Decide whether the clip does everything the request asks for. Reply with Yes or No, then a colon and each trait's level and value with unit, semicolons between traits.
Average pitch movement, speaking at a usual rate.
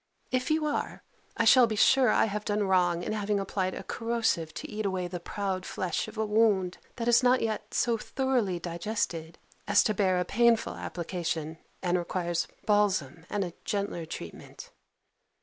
Yes: average, 4.1 semitones; average, 175 wpm